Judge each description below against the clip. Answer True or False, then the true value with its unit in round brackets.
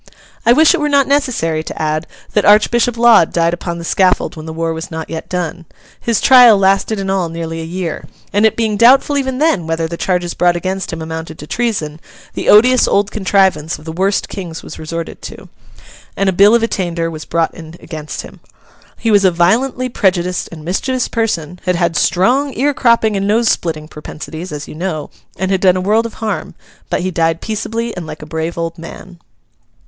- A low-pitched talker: False (185 Hz)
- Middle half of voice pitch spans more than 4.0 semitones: True (5.2 semitones)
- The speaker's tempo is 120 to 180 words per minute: False (205 wpm)